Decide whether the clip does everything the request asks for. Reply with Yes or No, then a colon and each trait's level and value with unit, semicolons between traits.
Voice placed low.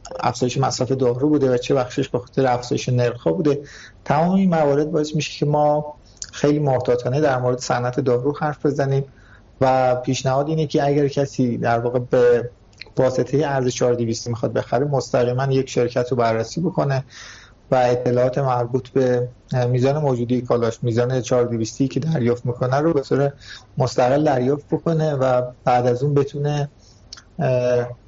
Yes: low, 130 Hz